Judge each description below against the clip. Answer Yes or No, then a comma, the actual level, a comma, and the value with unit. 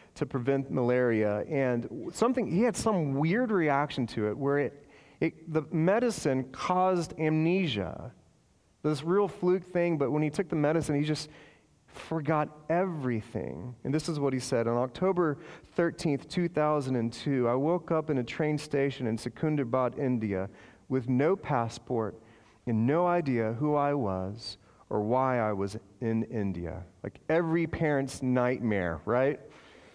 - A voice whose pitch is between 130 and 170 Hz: Yes, medium, 140 Hz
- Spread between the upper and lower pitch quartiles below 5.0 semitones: No, wide, 5.4 semitones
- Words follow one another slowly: No, average, 145 wpm